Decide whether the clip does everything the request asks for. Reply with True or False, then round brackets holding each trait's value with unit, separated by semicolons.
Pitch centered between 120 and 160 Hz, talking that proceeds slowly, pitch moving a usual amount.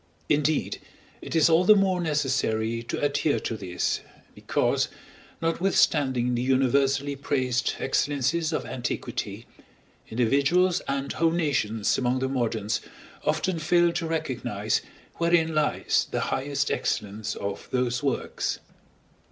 True (140 Hz; 120 wpm; 4.7 semitones)